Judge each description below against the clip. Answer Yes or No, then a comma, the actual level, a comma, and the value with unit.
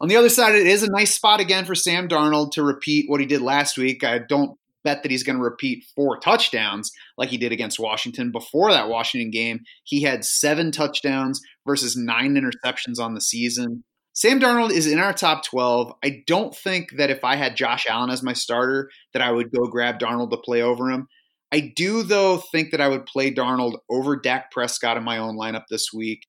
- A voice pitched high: No, low, 135 Hz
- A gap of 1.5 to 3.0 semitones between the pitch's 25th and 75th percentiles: No, average, 4.1 semitones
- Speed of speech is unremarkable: No, fast, 220 wpm